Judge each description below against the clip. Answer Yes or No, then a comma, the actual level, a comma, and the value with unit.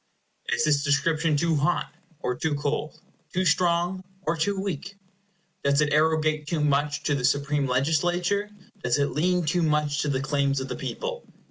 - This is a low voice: No, medium, 150 Hz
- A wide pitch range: No, average, 3.3 semitones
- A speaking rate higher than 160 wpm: Yes, average, 170 wpm